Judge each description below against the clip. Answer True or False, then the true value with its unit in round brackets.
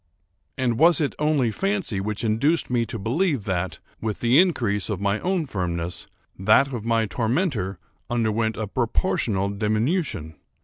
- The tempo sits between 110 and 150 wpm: True (145 wpm)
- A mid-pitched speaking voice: False (115 Hz)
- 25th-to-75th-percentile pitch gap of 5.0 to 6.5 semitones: True (5.6 semitones)